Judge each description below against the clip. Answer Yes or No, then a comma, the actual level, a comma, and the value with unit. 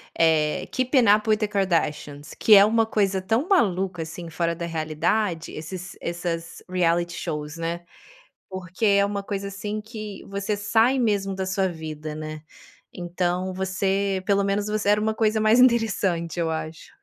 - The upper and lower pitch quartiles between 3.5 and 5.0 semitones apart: Yes, average, 3.8 semitones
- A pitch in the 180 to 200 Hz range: Yes, high, 190 Hz